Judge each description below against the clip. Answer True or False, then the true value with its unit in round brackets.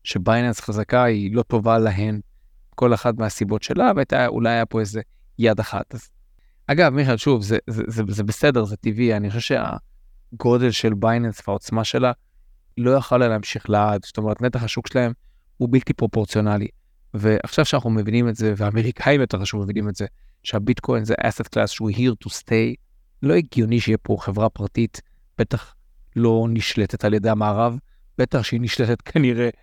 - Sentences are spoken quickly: True (165 wpm)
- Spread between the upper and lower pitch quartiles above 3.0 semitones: False (2.3 semitones)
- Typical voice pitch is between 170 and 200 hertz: False (115 Hz)